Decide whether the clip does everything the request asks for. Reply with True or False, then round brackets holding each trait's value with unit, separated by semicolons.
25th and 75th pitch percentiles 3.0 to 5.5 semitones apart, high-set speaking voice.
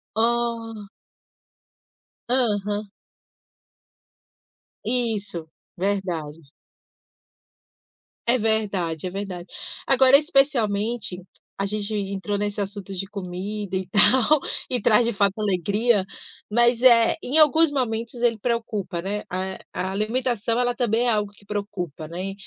True (3.4 semitones; 210 Hz)